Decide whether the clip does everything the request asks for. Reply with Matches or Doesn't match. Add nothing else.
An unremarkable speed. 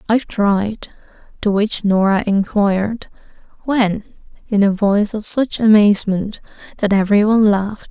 Doesn't match